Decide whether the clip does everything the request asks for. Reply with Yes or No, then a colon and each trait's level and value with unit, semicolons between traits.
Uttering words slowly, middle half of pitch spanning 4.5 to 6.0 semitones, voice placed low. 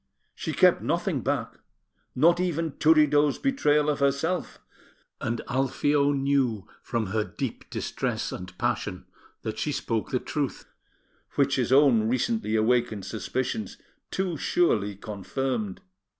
Yes: slow, 120 wpm; average, 5.2 semitones; low, 130 Hz